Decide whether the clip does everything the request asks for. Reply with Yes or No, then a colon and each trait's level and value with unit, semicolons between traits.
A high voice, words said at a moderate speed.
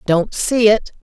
Yes: high, 210 Hz; average, 165 wpm